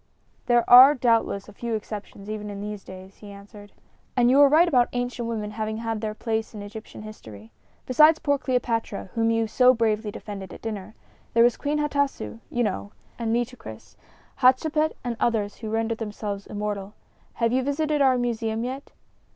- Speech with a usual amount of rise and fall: Yes, average, 3.1 semitones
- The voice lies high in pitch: Yes, high, 225 Hz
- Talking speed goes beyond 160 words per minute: Yes, average, 175 wpm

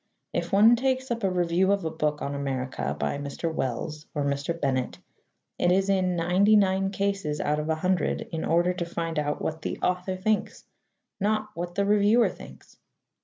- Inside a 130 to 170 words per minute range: No, average, 185 wpm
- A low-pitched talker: No, medium, 175 Hz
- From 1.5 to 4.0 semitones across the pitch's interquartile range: No, average, 4.5 semitones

